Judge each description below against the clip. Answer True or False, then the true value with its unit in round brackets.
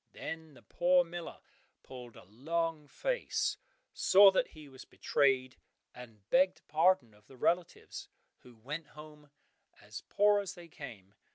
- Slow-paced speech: False (145 wpm)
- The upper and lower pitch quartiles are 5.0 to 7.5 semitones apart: True (5.6 semitones)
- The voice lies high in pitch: False (150 Hz)